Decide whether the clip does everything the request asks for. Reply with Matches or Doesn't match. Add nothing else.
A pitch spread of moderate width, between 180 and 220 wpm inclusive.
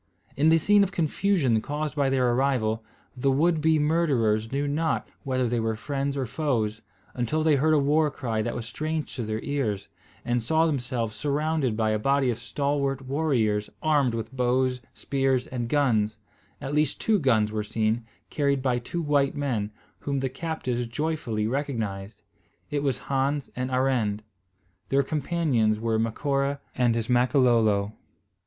Doesn't match